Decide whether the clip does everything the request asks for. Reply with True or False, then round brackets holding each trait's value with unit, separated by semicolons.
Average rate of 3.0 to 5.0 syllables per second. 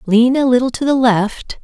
True (4.6 syllables/s)